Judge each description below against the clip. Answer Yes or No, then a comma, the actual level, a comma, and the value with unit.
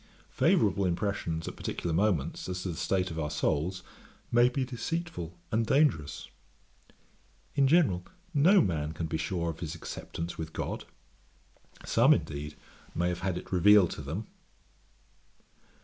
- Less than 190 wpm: Yes, average, 145 wpm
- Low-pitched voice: Yes, very low, 90 Hz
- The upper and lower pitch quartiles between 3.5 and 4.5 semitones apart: No, average, 5.1 semitones